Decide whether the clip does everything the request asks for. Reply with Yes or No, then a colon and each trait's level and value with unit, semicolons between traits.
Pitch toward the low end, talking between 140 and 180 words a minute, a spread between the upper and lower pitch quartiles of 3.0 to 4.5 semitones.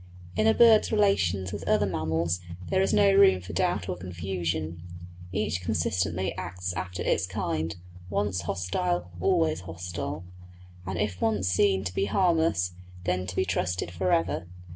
No: very low, 90 Hz; average, 155 wpm; narrow, 2.6 semitones